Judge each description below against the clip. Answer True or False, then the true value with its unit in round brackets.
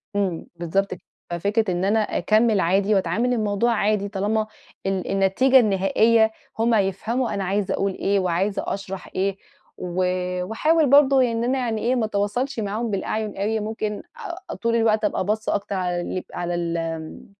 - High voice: True (205 Hz)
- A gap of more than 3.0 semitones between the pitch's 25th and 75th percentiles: False (2.7 semitones)